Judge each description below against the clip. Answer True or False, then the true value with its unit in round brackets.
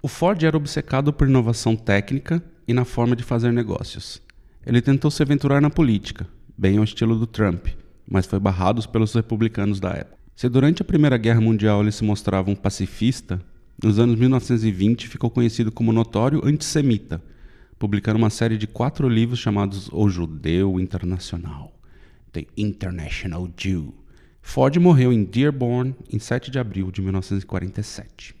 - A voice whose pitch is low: True (110 Hz)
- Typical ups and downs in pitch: True (4.4 semitones)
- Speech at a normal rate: True (155 wpm)